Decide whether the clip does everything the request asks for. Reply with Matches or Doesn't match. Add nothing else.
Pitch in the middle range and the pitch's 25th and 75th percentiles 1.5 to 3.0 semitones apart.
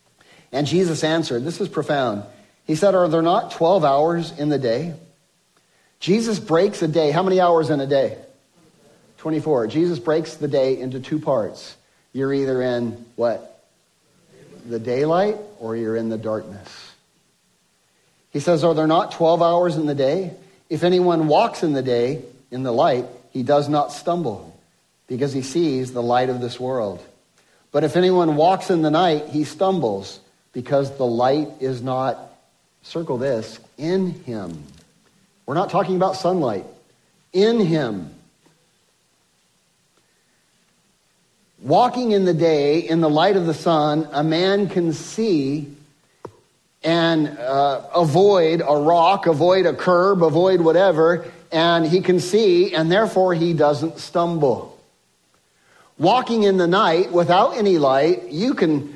Doesn't match